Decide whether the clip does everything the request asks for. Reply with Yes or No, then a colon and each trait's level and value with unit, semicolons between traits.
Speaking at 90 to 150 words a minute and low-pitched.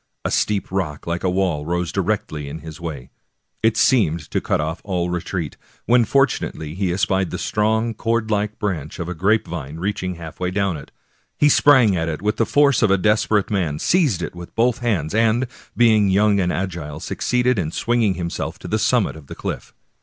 No: average, 200 wpm; very low, 95 Hz